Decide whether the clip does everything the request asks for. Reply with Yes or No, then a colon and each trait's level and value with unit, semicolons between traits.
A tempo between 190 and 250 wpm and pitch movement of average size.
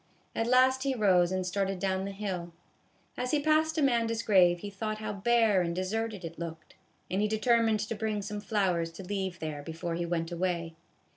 Yes: average, 195 wpm; average, 4.2 semitones